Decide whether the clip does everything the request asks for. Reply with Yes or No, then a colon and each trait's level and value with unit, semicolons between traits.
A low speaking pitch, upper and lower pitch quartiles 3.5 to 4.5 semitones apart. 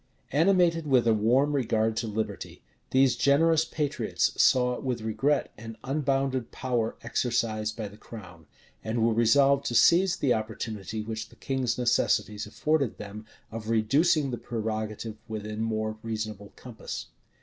Yes: low, 115 Hz; average, 3.9 semitones